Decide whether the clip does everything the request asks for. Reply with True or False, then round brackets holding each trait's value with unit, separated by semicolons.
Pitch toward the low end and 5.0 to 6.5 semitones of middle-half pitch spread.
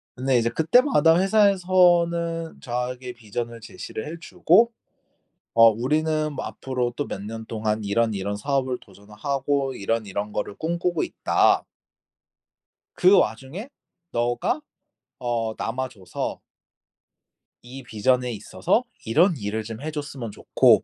True (125 Hz; 6.2 semitones)